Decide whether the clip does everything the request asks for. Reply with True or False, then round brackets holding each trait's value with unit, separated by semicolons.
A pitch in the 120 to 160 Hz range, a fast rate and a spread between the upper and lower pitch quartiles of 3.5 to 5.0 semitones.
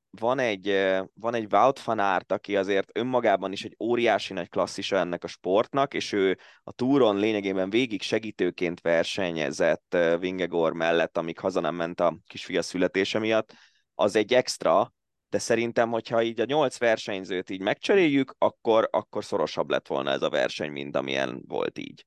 False (95 Hz; 165 wpm; 4.2 semitones)